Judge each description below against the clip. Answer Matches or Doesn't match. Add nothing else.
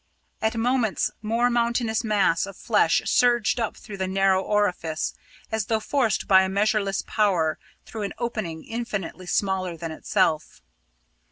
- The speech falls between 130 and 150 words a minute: Matches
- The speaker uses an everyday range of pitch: Matches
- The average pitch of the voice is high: Matches